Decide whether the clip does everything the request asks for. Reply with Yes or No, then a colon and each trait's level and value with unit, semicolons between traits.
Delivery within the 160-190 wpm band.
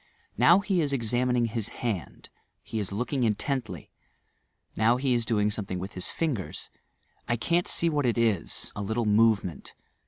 Yes: average, 165 wpm